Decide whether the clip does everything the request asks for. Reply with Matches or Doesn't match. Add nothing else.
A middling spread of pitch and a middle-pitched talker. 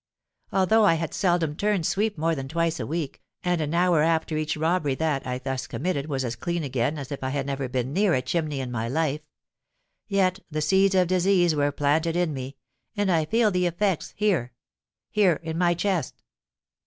Matches